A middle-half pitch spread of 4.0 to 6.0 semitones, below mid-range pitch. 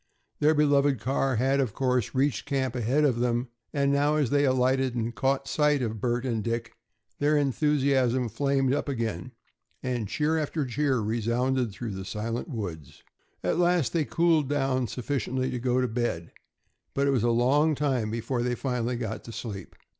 No: average, 3.2 semitones; low, 130 Hz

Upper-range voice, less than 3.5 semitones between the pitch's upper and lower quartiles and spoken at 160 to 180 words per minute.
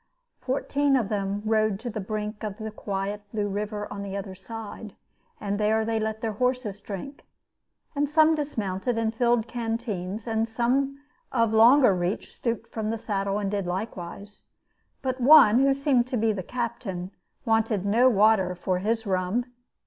Yes: high, 220 Hz; average, 3.0 semitones; average, 165 wpm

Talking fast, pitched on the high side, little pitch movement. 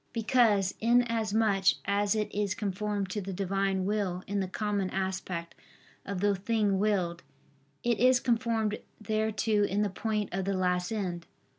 No: average, 150 wpm; high, 205 Hz; narrow, 2.3 semitones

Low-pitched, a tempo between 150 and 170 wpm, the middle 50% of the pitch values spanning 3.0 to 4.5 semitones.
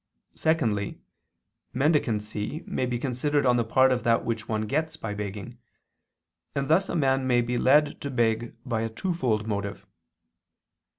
Yes: low, 120 Hz; average, 155 wpm; average, 4.2 semitones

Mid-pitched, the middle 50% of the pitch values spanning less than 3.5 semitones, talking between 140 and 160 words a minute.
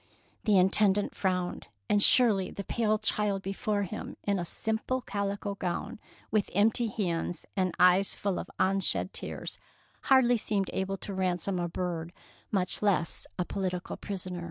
No: high, 195 Hz; narrow, 2.4 semitones; average, 150 wpm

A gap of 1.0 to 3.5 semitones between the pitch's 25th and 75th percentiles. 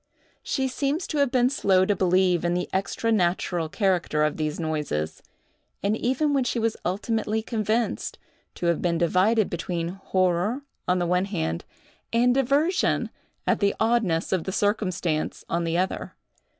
No: average, 5.0 semitones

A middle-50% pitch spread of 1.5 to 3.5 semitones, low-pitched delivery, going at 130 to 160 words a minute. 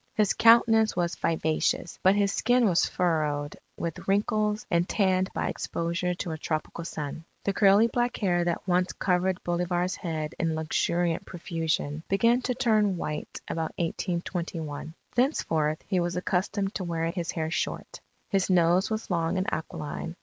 No: average, 3.2 semitones; medium, 175 Hz; average, 155 wpm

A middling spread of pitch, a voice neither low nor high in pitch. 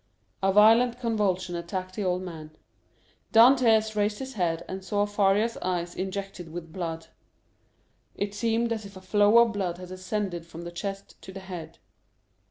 No: average, 3.3 semitones; high, 195 Hz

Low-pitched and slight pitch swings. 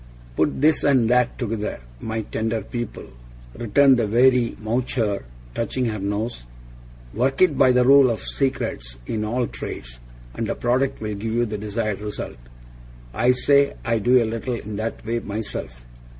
No: low, 115 Hz; average, 3.0 semitones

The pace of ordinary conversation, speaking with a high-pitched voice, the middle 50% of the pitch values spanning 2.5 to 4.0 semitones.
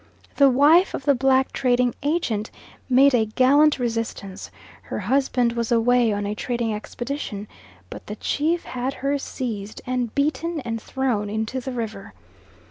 Yes: average, 150 wpm; high, 245 Hz; average, 3.7 semitones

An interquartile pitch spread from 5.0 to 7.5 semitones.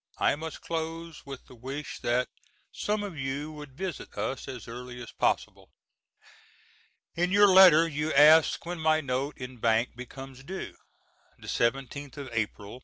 No: average, 4.3 semitones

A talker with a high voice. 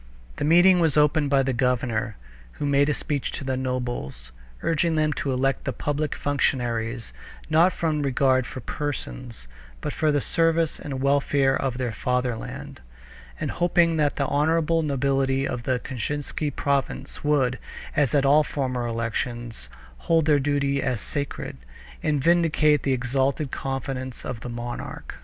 No: low, 135 Hz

